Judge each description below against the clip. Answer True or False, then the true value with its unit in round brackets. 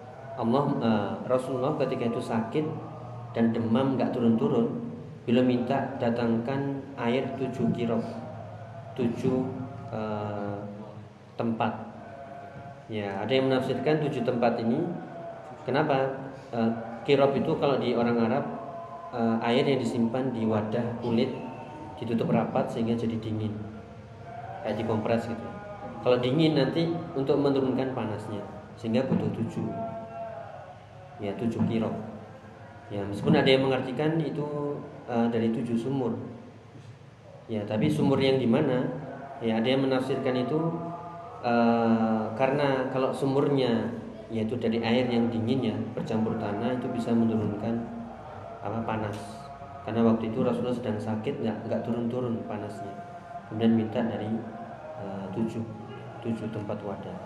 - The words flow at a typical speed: True (125 wpm)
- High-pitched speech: False (120 Hz)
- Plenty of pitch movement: False (2.9 semitones)